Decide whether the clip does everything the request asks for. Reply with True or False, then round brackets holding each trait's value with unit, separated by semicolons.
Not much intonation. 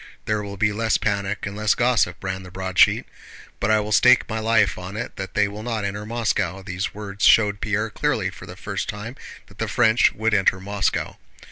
True (2.0 semitones)